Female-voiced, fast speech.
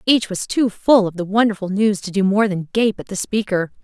Yes: female; fast, 250 wpm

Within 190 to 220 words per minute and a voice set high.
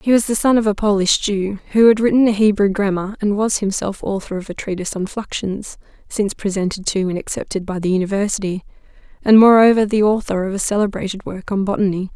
Yes: average, 200 wpm; high, 200 Hz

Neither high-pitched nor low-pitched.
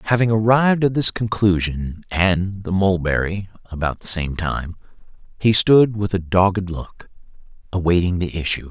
No: very low, 95 Hz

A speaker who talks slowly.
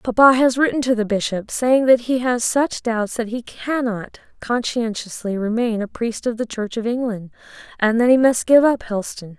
No: average, 200 wpm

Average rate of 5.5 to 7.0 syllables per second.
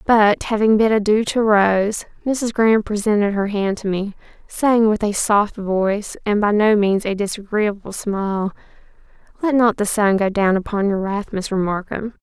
No: 4.5 syllables/s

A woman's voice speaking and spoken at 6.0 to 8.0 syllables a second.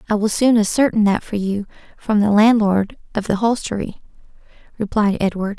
No: female; 5.3 syllables/s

